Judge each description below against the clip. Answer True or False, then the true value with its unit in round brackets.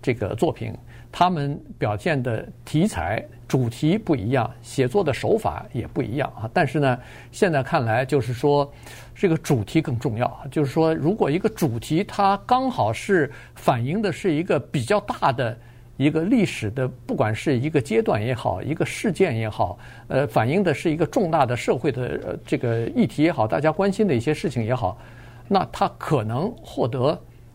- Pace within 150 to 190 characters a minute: False (265 characters per minute)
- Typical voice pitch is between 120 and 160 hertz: True (140 Hz)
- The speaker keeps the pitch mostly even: False (5.5 semitones)